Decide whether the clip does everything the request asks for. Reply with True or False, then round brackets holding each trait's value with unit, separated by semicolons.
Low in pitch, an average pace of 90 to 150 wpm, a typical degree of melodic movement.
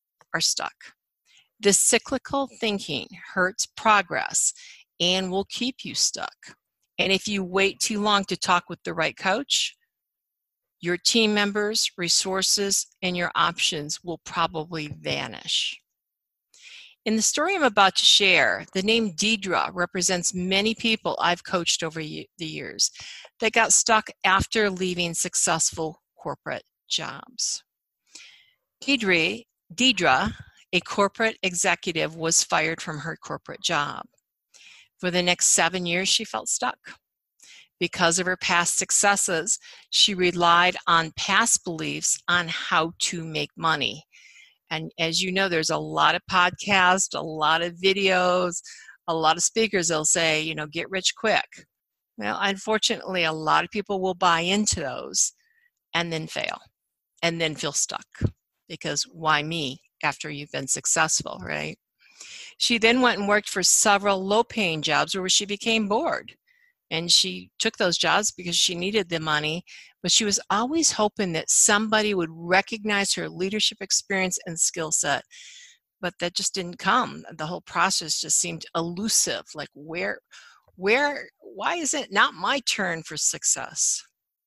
False (185 Hz; 145 wpm; 4.1 semitones)